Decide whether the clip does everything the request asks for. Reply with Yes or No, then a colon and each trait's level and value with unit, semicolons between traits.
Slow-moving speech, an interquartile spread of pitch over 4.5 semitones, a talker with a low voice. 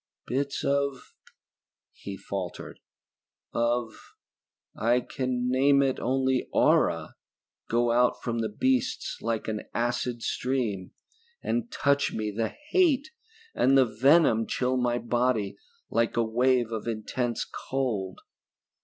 No: slow, 125 wpm; average, 2.8 semitones; low, 125 Hz